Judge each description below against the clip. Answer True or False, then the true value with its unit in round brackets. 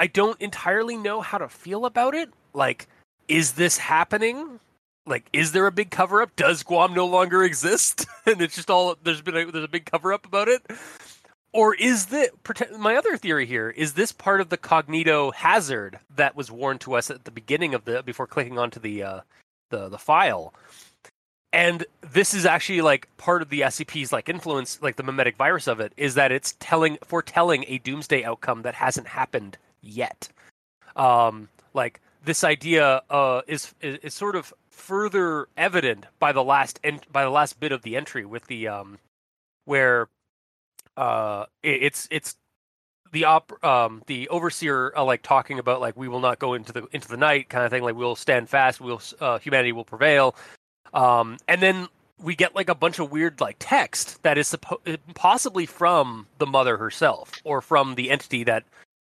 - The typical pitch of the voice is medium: True (155 Hz)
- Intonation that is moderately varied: False (5.7 semitones)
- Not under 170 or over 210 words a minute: True (190 wpm)